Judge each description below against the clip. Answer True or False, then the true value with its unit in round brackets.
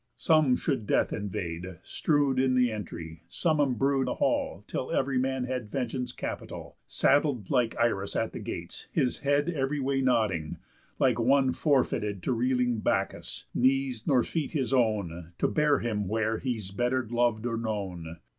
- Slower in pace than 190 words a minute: True (160 wpm)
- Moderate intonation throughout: True (4.0 semitones)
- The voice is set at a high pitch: False (125 Hz)